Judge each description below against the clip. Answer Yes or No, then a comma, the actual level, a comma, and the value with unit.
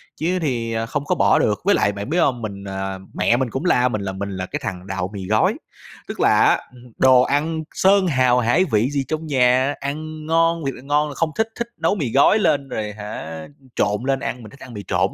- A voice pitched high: No, low, 130 Hz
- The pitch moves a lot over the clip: Yes, wide, 6.6 semitones